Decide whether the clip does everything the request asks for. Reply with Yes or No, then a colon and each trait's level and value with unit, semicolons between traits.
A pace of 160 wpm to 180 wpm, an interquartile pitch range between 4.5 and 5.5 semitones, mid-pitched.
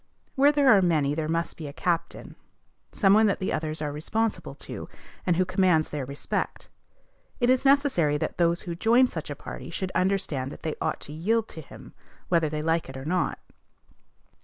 No: average, 195 wpm; average, 5.2 semitones; medium, 170 Hz